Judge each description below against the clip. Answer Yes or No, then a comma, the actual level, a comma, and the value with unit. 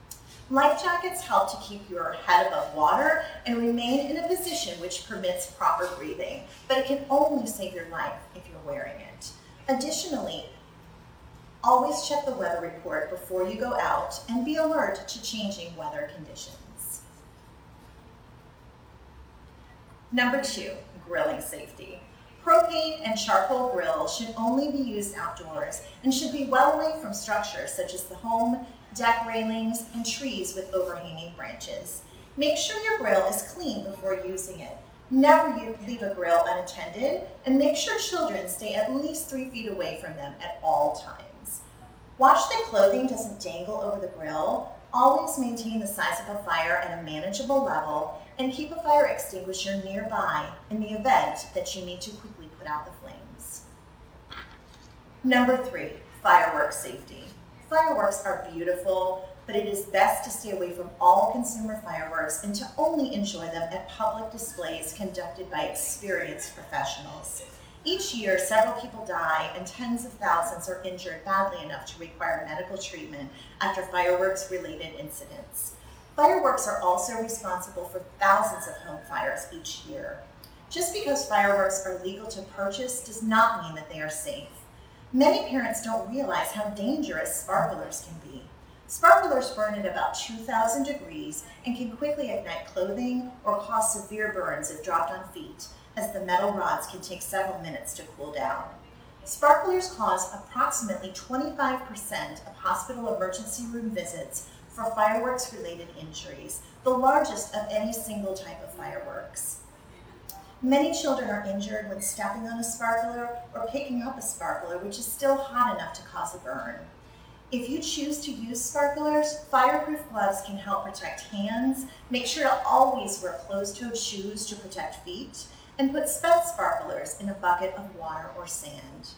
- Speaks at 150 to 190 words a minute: Yes, average, 155 wpm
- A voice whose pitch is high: Yes, high, 225 Hz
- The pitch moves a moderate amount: No, wide, 6.4 semitones